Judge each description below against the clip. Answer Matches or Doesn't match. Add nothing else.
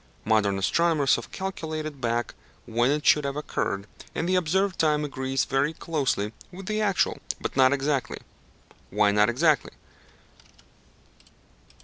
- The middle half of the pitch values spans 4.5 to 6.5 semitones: Matches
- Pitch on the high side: Doesn't match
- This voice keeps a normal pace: Doesn't match